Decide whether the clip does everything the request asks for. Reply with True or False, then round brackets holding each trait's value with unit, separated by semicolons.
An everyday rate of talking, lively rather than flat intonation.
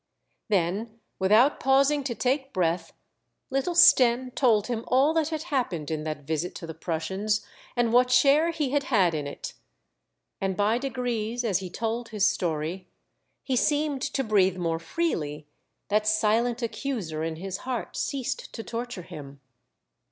True (155 wpm; 6.5 semitones)